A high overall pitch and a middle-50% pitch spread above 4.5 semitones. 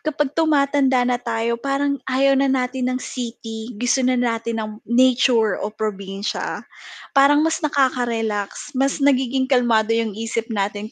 No: high, 245 Hz; average, 3.3 semitones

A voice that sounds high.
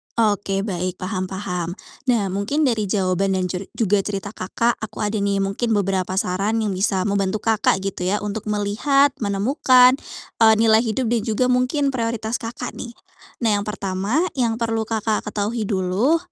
Yes: high, 210 Hz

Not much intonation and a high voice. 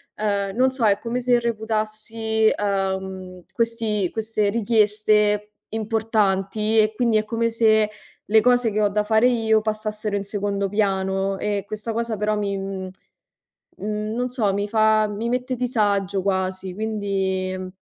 Yes: narrow, 2.0 semitones; high, 215 Hz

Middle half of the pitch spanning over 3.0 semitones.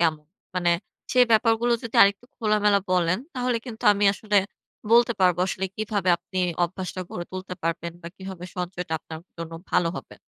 Yes: average, 3.5 semitones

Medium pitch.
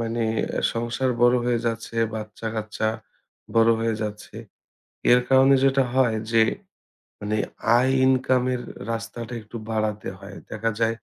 No: low, 115 Hz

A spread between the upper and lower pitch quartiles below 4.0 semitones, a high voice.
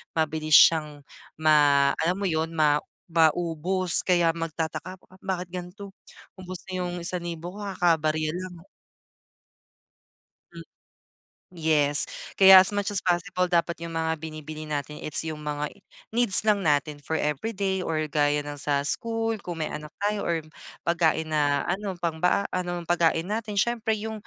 No: average, 3.2 semitones; medium, 170 Hz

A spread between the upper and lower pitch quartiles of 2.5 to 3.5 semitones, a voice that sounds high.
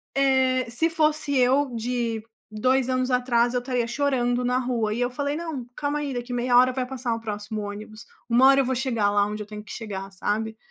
Yes: average, 2.9 semitones; high, 245 Hz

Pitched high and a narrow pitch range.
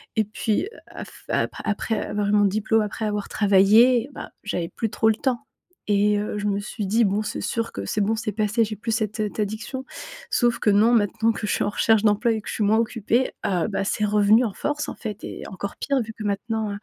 Yes: high, 215 Hz; narrow, 1.6 semitones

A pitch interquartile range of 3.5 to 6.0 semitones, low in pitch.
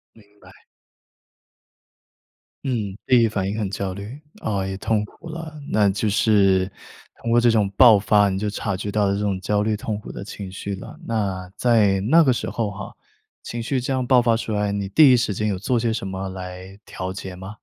No: average, 2.9 semitones; low, 105 Hz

